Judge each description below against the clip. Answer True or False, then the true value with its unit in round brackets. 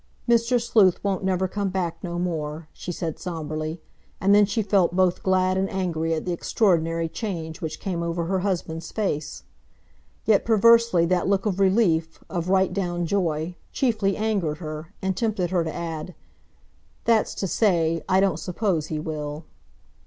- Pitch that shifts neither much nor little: True (3.3 semitones)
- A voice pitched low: False (180 Hz)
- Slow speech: False (165 wpm)